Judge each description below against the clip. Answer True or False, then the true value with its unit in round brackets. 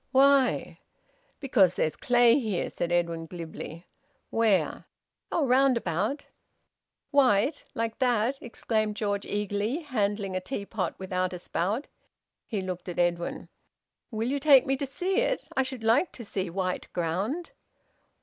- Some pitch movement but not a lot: False (6.2 semitones)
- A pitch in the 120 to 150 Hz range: False (215 Hz)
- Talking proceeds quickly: False (140 wpm)